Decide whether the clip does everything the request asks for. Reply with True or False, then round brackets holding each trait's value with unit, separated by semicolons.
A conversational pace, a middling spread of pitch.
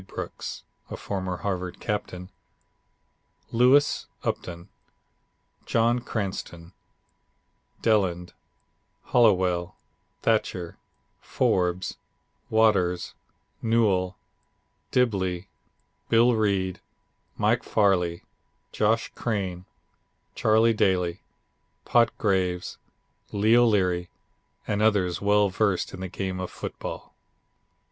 False (80 wpm; 3.4 semitones)